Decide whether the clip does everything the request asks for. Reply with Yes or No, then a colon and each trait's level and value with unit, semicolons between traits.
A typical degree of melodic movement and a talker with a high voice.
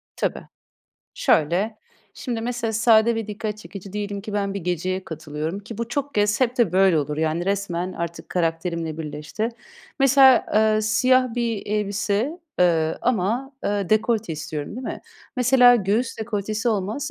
Yes: average, 4.5 semitones; high, 210 Hz